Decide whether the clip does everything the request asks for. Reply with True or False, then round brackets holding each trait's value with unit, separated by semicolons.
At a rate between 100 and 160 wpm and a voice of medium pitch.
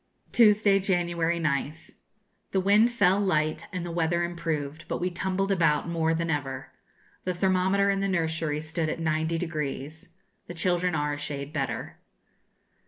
True (150 wpm; 170 Hz)